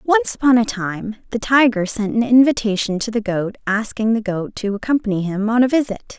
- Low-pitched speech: No, high, 225 Hz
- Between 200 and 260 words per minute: Yes, fast, 205 wpm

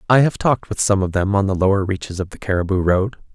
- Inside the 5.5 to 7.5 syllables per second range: Yes, 6.6 syllables/s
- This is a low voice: Yes, low, 100 Hz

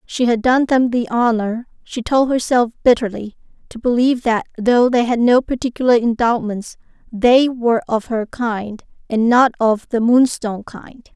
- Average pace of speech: Yes, average, 160 wpm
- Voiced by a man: No, female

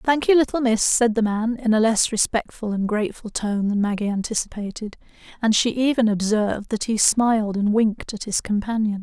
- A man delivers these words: No, female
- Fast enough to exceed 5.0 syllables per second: Yes, 5.4 syllables/s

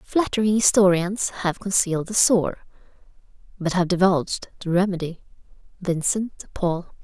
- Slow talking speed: Yes, slow, 120 wpm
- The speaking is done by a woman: Yes, female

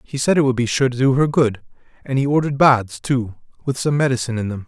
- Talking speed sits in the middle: No, fast, 255 wpm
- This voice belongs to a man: Yes, male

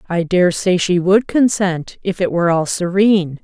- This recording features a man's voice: No, female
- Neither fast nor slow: Yes, average, 175 wpm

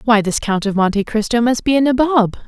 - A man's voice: No, female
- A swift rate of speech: Yes, fast, 240 wpm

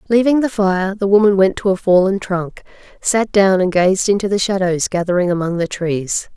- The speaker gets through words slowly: No, average, 200 wpm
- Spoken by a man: No, female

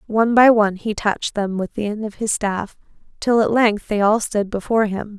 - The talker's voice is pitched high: Yes, high, 210 Hz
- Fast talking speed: Yes, fast, 230 wpm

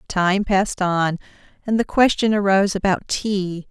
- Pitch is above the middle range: Yes, high, 195 Hz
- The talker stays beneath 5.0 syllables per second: Yes, 4.6 syllables/s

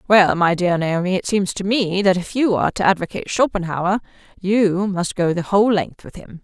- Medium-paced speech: No, fast, 215 wpm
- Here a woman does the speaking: Yes, female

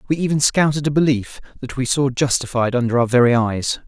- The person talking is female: No, male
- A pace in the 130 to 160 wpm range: No, average, 200 wpm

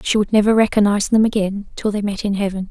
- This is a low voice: No, high, 205 Hz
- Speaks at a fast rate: Yes, fast, 245 wpm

